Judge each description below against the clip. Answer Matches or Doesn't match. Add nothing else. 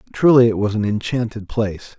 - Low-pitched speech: Matches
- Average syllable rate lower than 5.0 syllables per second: Doesn't match